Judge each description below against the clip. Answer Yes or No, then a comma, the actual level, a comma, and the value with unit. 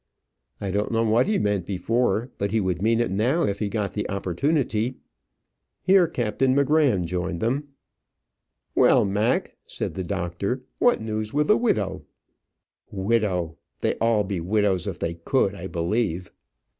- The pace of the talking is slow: No, average, 155 wpm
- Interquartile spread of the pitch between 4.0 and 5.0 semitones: Yes, average, 4.4 semitones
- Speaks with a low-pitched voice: Yes, low, 105 Hz